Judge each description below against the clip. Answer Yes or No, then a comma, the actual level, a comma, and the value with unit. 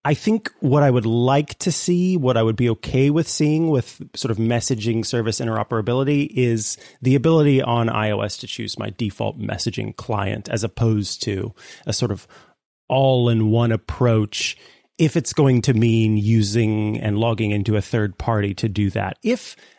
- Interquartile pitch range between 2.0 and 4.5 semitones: Yes, average, 3.5 semitones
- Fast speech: No, average, 175 wpm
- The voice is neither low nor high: No, low, 115 Hz